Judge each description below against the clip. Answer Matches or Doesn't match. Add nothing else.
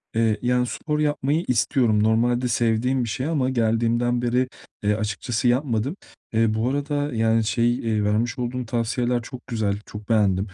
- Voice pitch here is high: Doesn't match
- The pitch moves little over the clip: Matches